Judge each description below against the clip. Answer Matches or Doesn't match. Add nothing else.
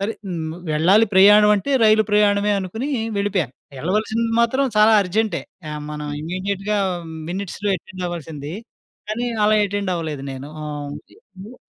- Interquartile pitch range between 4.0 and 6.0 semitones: Matches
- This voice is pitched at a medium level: Doesn't match